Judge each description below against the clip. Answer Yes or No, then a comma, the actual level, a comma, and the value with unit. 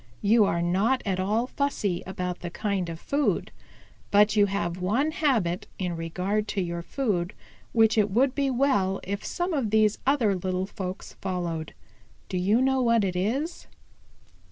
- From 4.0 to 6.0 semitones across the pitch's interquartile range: Yes, average, 4.8 semitones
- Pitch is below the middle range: No, high, 200 Hz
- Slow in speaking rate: No, average, 165 wpm